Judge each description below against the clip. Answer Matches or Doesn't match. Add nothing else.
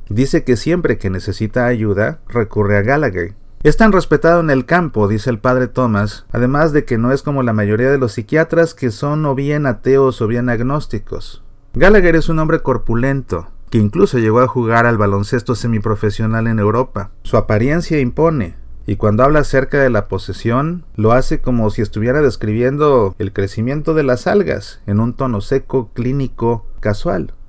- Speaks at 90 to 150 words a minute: Doesn't match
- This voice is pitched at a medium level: Doesn't match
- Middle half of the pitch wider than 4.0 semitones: Matches